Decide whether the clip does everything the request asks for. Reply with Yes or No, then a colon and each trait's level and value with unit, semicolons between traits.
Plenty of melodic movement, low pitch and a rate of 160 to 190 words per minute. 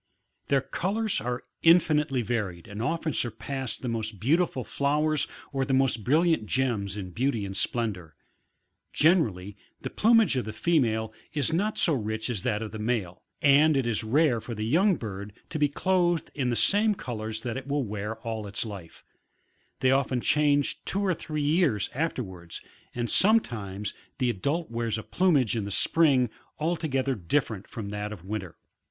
Yes: wide, 6.0 semitones; low, 125 Hz; average, 170 wpm